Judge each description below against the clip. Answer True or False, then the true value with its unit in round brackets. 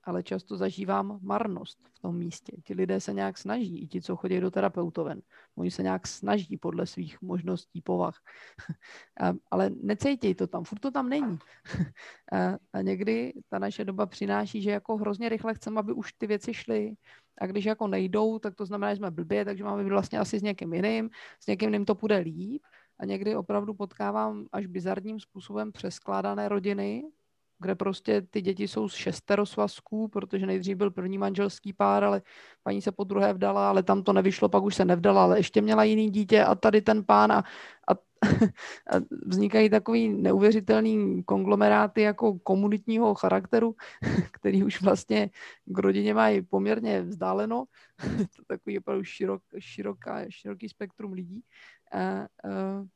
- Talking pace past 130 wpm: True (165 wpm)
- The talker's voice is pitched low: False (195 Hz)